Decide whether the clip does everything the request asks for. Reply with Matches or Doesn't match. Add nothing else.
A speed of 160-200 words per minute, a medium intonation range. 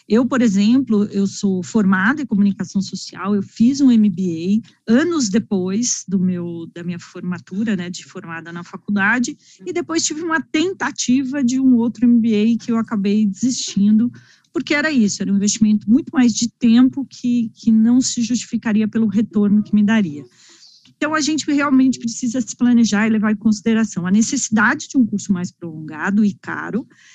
Matches